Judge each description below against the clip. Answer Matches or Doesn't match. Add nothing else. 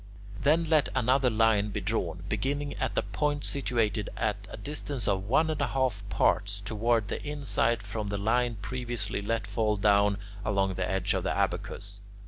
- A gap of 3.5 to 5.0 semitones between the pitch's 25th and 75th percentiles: Matches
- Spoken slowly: Doesn't match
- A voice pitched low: Matches